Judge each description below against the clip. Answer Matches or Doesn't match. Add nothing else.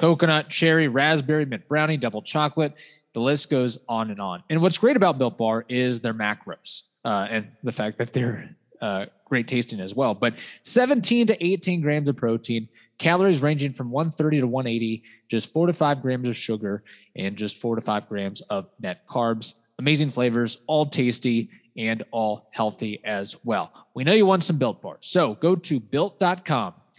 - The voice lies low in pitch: Matches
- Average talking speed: Matches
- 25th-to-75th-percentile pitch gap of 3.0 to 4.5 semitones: Doesn't match